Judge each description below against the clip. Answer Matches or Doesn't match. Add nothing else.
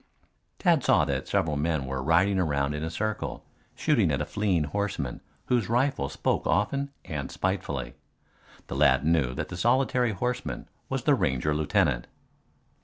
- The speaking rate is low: Doesn't match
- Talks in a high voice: Doesn't match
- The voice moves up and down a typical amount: Doesn't match